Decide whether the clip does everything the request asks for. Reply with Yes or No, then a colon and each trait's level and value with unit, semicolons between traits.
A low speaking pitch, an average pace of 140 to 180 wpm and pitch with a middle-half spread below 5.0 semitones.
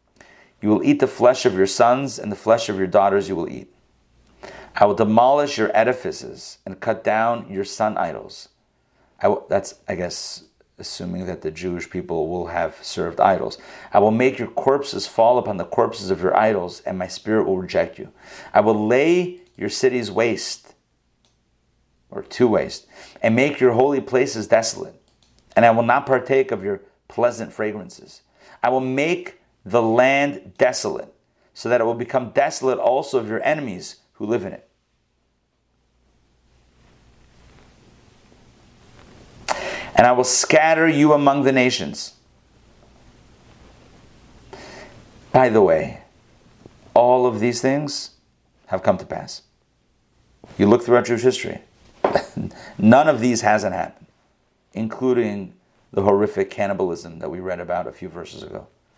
Yes: low, 120 Hz; average, 150 wpm; average, 4.4 semitones